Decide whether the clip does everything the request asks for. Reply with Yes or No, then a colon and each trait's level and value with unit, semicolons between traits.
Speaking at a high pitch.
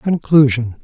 No: low, 135 Hz